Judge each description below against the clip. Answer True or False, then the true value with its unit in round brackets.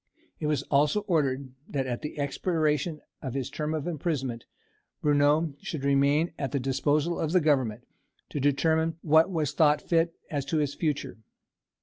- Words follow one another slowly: False (160 wpm)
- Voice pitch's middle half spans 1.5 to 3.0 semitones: True (2.5 semitones)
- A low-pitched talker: False (150 Hz)